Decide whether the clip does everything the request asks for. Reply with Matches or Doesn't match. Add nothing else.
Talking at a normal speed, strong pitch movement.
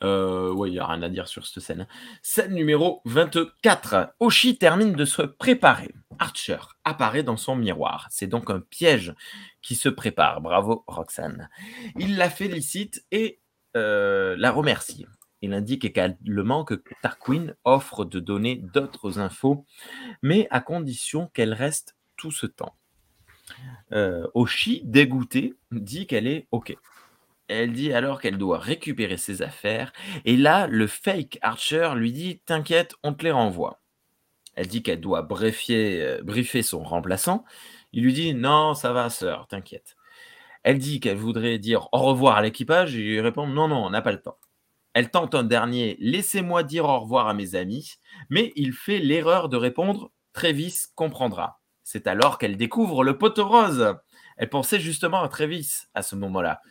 Matches